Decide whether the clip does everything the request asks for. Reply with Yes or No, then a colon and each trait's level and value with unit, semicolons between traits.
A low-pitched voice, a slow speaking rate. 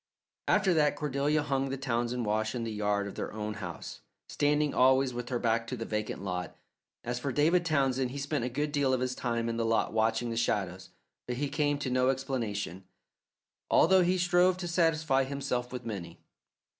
No: low, 130 Hz; average, 195 wpm